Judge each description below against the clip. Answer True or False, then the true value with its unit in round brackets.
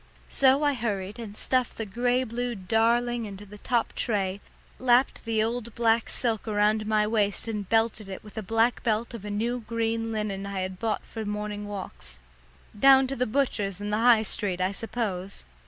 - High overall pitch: True (220 Hz)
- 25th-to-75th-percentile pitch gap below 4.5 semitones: True (2.4 semitones)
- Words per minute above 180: True (190 wpm)